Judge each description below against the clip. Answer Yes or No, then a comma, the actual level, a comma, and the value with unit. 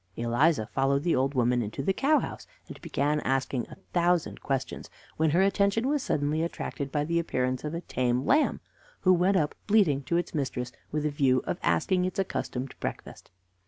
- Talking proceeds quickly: No, average, 190 wpm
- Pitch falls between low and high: Yes, medium, 150 Hz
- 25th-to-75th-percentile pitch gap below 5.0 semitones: No, average, 5.3 semitones